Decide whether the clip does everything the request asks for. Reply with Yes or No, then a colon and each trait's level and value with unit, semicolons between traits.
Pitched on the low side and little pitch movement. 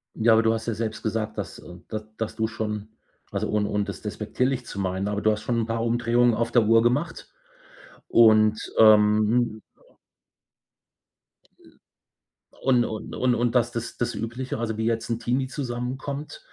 Yes: low, 115 Hz; narrow, 2.0 semitones